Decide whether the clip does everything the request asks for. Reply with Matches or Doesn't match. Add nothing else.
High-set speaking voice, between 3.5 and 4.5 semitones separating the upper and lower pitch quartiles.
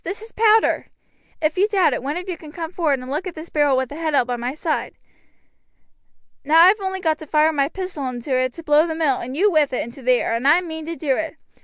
Matches